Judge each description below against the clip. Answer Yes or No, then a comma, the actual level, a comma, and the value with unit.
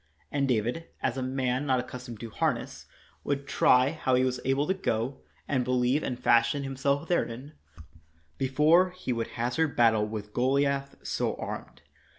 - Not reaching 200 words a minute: Yes, average, 160 wpm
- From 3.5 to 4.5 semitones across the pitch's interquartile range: No, narrow, 2.5 semitones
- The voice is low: Yes, low, 130 Hz